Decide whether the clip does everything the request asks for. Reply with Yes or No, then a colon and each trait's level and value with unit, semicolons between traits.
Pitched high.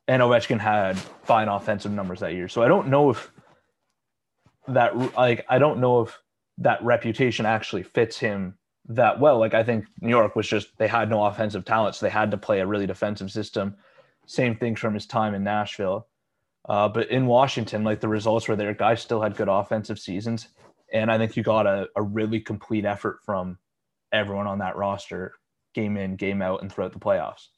No: low, 110 Hz